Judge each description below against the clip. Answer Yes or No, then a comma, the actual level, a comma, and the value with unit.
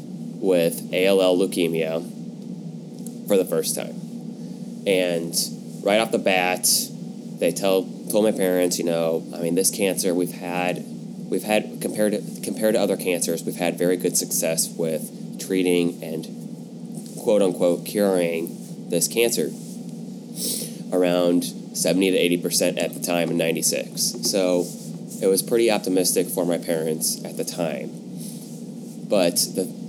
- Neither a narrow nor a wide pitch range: No, narrow, 1.7 semitones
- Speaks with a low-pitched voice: Yes, very low, 90 Hz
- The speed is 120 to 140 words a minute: Yes, slow, 135 wpm